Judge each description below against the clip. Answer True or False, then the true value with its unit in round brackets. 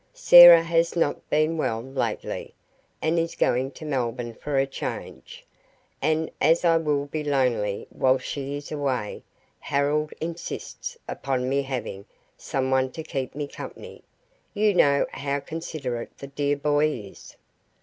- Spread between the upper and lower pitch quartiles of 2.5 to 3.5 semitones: True (3.2 semitones)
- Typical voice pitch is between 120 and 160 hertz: True (140 Hz)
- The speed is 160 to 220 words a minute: False (140 wpm)